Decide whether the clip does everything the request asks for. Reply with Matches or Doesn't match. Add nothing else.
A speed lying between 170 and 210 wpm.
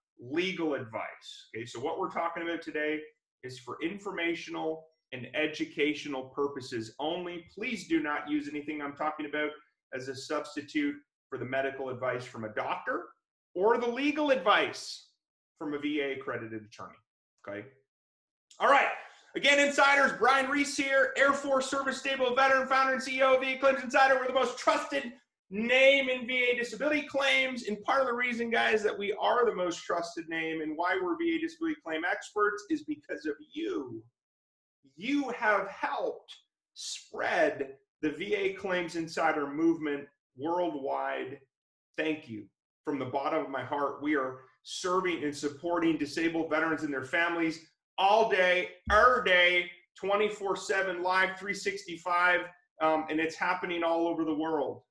Doesn't match